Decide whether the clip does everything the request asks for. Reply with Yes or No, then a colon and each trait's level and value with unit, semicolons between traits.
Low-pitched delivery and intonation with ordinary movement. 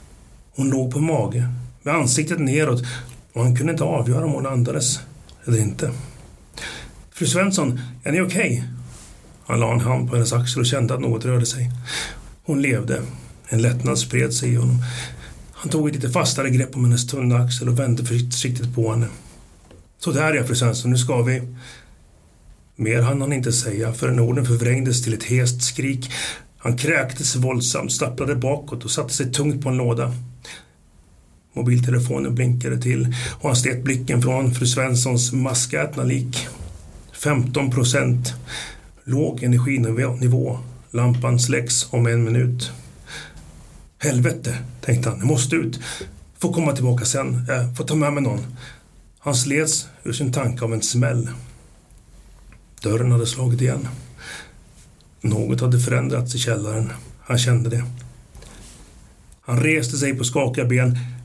No: low, 125 Hz; narrow, 2.0 semitones